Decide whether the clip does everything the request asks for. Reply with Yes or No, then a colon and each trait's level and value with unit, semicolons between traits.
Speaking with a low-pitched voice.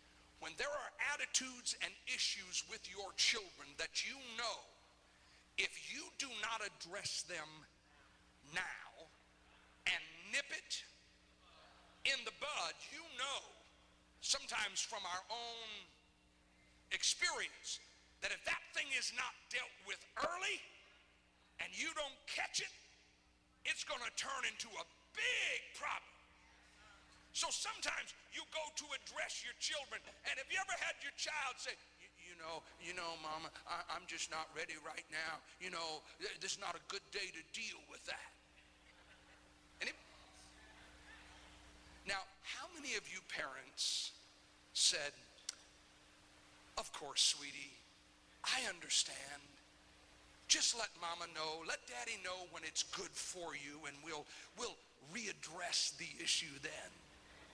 Yes: very low, 75 Hz